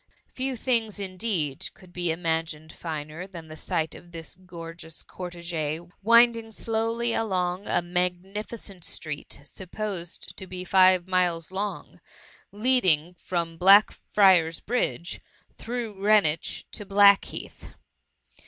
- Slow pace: Yes, slow, 110 wpm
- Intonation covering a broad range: No, average, 3.8 semitones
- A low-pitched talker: No, medium, 185 Hz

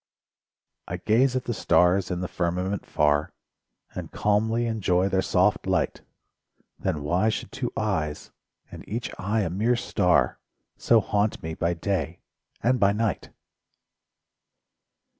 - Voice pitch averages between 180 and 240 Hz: No, low, 100 Hz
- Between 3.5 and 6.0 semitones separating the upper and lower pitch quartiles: Yes, average, 4.0 semitones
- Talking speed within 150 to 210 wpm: No, slow, 135 wpm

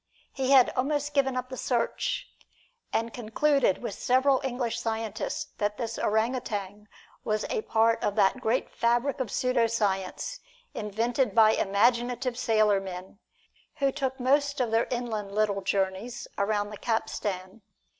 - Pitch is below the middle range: No, high, 230 Hz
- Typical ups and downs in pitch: Yes, average, 3.6 semitones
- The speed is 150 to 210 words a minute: No, average, 140 wpm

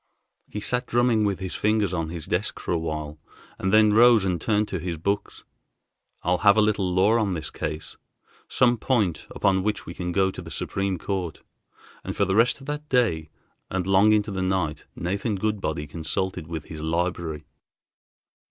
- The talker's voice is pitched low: Yes, very low, 95 Hz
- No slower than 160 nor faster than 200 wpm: Yes, average, 185 wpm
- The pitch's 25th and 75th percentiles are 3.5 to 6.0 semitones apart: Yes, average, 4.1 semitones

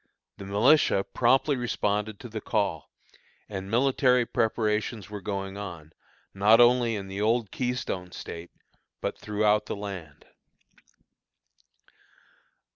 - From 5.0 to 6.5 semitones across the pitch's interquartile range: No, average, 3.4 semitones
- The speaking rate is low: Yes, slow, 115 wpm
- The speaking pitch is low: Yes, low, 105 Hz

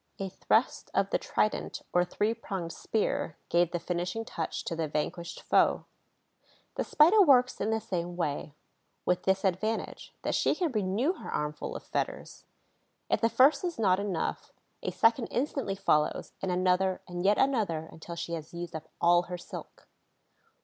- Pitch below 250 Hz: Yes, medium, 185 Hz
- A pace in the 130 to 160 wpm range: No, average, 170 wpm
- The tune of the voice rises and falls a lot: No, average, 4.7 semitones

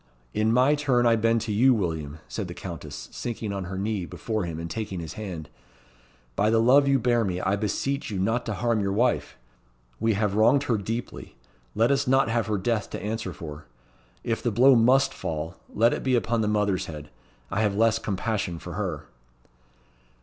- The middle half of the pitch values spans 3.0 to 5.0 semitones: Yes, average, 3.7 semitones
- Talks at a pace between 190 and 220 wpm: Yes, average, 200 wpm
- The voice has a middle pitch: No, low, 110 Hz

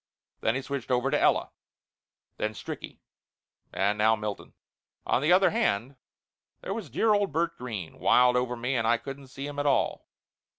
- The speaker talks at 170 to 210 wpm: Yes, average, 175 wpm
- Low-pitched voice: Yes, low, 130 Hz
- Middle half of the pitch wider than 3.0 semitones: Yes, average, 4.2 semitones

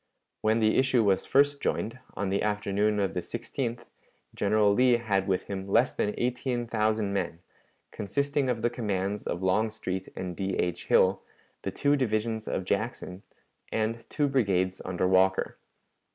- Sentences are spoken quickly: No, average, 155 wpm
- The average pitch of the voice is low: Yes, low, 105 Hz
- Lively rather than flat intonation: No, average, 3.7 semitones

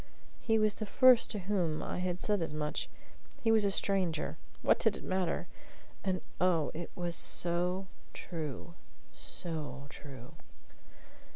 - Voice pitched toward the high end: No, medium, 180 Hz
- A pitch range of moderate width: Yes, average, 3.6 semitones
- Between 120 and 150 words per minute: Yes, average, 145 wpm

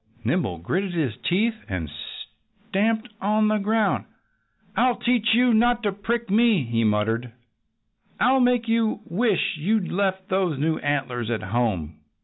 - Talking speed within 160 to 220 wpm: No, average, 140 wpm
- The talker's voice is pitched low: No, high, 195 Hz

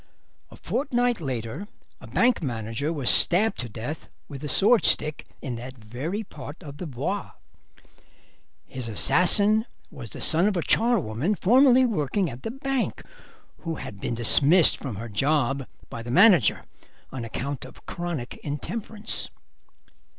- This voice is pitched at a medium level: Yes, medium, 150 Hz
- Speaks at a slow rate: No, average, 145 wpm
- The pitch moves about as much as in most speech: No, wide, 8.8 semitones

